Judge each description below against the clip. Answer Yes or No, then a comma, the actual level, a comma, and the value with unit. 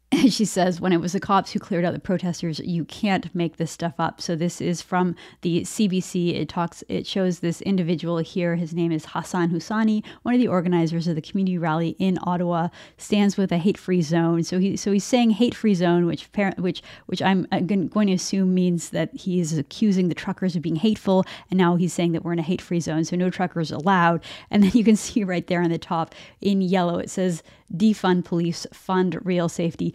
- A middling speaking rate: No, fast, 220 wpm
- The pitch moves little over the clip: Yes, narrow, 2.2 semitones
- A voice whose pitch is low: No, medium, 180 Hz